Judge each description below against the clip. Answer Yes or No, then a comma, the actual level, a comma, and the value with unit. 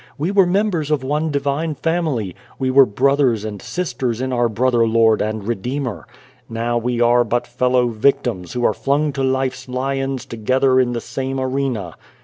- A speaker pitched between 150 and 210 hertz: No, low, 130 Hz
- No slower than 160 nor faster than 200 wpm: Yes, average, 170 wpm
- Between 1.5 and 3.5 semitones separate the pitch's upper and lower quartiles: Yes, average, 2.8 semitones